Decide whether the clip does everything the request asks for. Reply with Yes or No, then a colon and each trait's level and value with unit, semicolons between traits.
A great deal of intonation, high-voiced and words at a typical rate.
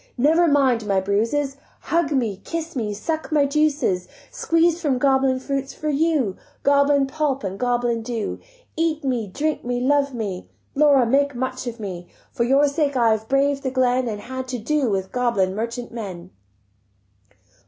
No: average, 4.0 semitones; very high, 260 Hz; average, 165 wpm